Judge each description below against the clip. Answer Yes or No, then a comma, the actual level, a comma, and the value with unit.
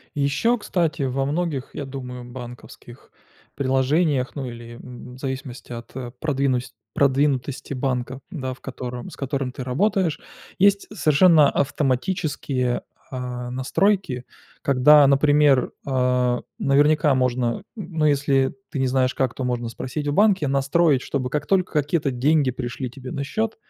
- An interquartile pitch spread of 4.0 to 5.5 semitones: No, average, 2.9 semitones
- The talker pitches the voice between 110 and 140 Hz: Yes, low, 135 Hz